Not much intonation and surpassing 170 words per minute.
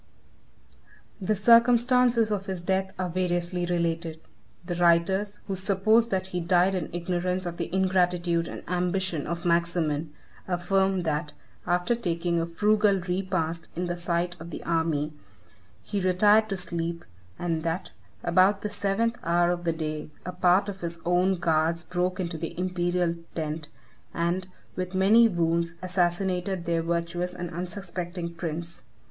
No: narrow, 2.0 semitones; average, 145 wpm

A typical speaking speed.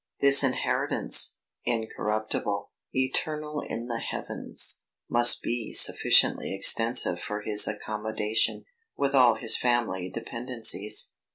No: slow, 100 wpm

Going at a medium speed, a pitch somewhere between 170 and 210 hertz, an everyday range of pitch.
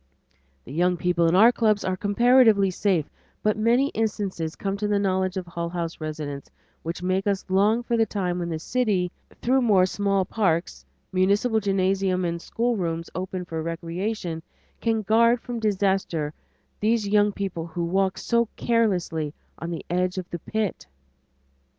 Yes: average, 160 wpm; high, 190 Hz; average, 3.8 semitones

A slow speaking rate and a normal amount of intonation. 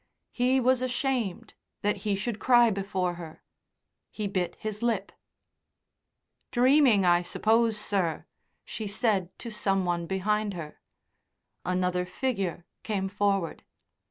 Yes: slow, 120 wpm; average, 4.3 semitones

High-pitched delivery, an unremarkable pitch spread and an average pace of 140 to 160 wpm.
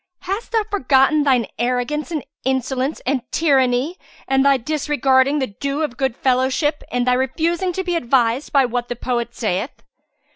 Yes: very high, 265 Hz; average, 3.3 semitones; average, 155 wpm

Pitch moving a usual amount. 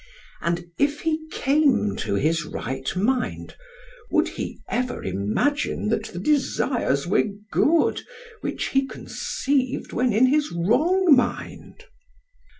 No: wide, 9.0 semitones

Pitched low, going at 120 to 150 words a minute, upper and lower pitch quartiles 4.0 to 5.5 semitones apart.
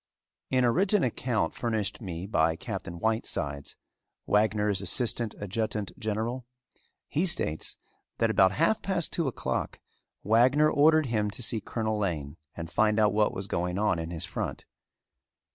Yes: low, 110 Hz; average, 145 wpm; average, 4.3 semitones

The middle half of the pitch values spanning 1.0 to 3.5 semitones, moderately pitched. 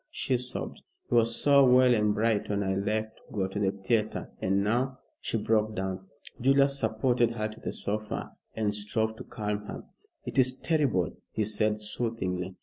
No: average, 2.9 semitones; low, 110 Hz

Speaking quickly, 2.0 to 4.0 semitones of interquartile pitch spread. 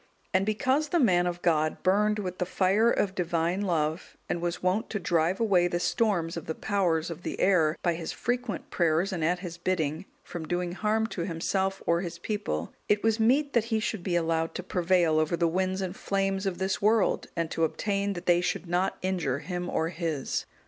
Yes: fast, 210 wpm; average, 3.0 semitones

